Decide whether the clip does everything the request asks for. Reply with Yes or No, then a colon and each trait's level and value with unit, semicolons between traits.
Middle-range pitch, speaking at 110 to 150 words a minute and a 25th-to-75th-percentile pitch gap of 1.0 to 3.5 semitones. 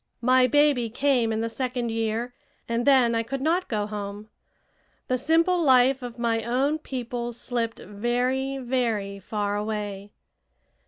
No: high, 240 Hz; average, 145 wpm; average, 2.9 semitones